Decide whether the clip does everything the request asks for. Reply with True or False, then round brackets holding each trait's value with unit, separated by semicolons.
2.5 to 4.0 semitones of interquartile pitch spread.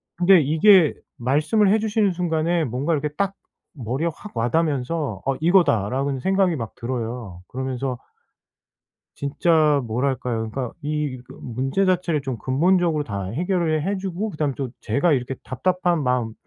False (5.6 semitones)